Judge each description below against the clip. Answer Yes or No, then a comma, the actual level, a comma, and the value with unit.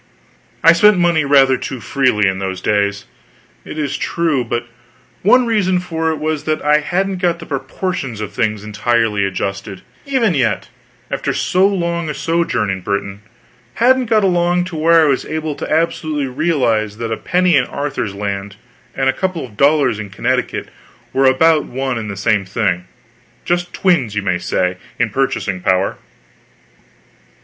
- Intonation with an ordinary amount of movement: No, wide, 8.2 semitones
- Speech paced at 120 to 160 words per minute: No, average, 170 wpm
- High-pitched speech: No, low, 135 Hz